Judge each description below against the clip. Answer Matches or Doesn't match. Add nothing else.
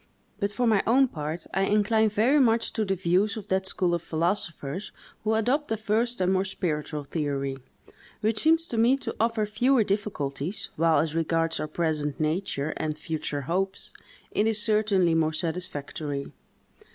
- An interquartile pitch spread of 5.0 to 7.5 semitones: Matches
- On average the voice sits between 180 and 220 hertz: Matches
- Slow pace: Doesn't match